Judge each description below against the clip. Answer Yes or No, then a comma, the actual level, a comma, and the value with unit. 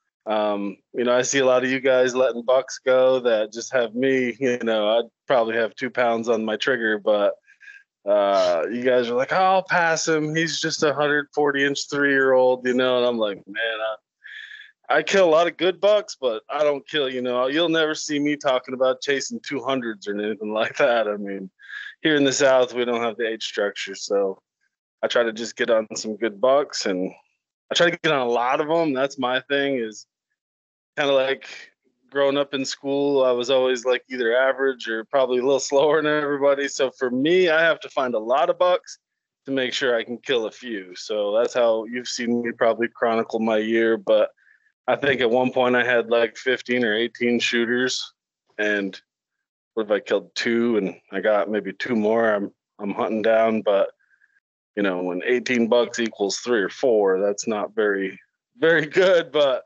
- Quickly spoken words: Yes, fast, 210 wpm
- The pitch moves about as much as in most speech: Yes, average, 4.1 semitones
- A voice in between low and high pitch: No, low, 125 Hz